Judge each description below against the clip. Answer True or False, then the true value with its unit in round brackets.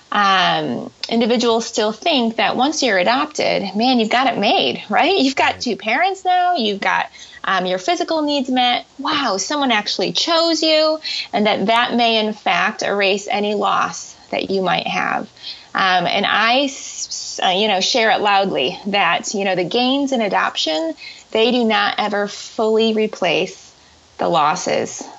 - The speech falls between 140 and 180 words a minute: True (160 wpm)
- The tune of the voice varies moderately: False (5.9 semitones)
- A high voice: True (235 Hz)